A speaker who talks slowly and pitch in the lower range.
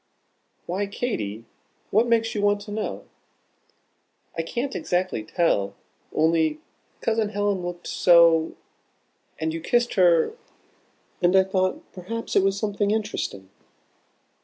No: slow, 120 wpm; high, 190 Hz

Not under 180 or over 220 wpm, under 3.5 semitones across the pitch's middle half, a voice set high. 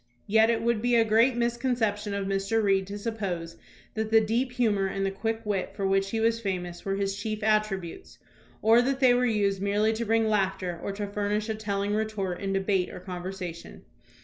Yes: average, 200 wpm; narrow, 2.4 semitones; high, 210 Hz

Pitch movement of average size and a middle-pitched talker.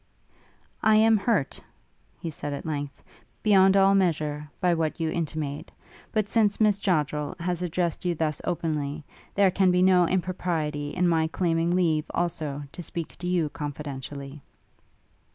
Yes: average, 3.5 semitones; medium, 165 Hz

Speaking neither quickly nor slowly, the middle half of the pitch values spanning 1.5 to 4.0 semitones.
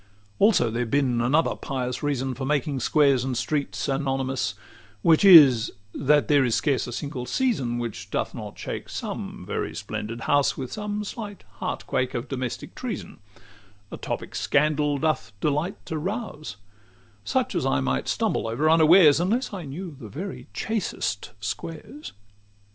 No: average, 155 wpm; average, 4.8 semitones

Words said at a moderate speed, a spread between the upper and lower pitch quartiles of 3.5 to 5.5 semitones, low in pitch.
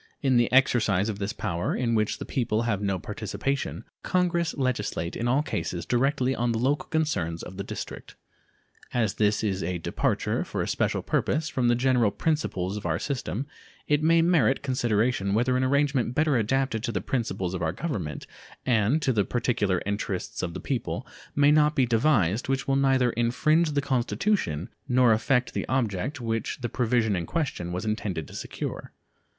Yes: average, 180 wpm; average, 5.0 semitones; low, 120 Hz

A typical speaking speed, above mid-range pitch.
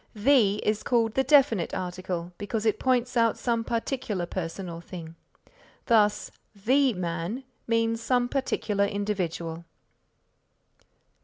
No: slow, 115 wpm; high, 215 Hz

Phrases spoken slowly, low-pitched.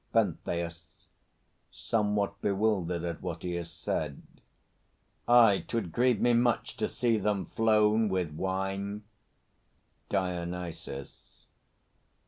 Yes: slow, 100 wpm; low, 100 Hz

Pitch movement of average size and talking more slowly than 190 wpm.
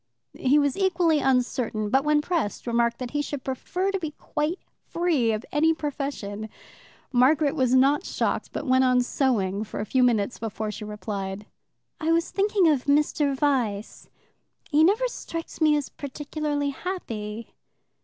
Yes: average, 4.8 semitones; average, 155 wpm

